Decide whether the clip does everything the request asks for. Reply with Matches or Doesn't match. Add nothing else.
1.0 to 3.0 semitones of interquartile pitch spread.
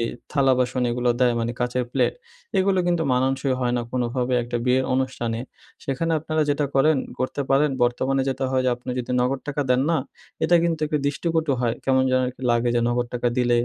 Matches